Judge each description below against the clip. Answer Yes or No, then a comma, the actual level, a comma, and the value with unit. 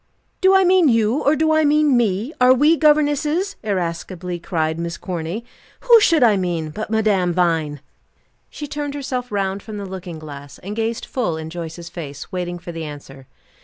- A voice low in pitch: No, high, 200 Hz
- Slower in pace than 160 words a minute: No, average, 180 wpm